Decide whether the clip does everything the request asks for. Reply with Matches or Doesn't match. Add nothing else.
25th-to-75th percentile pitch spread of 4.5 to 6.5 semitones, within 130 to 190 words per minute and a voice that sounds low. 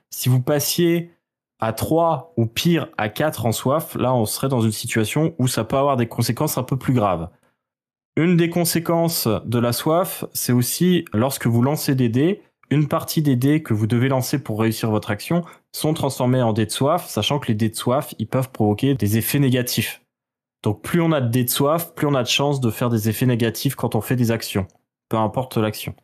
Doesn't match